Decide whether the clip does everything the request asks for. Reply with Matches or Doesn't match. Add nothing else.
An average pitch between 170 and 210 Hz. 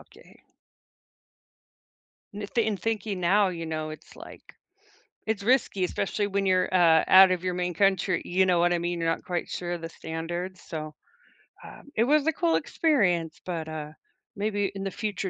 Matches